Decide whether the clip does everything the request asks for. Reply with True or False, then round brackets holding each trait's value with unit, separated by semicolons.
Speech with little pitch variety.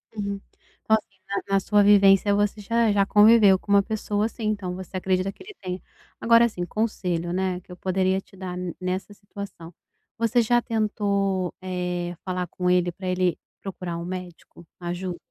True (2.3 semitones)